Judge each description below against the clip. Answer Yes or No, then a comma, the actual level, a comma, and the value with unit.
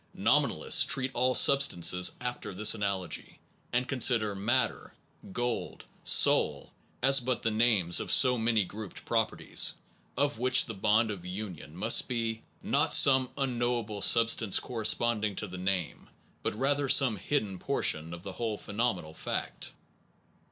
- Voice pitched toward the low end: Yes, low, 110 Hz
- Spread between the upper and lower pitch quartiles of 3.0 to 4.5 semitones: Yes, average, 4.0 semitones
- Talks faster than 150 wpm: No, slow, 135 wpm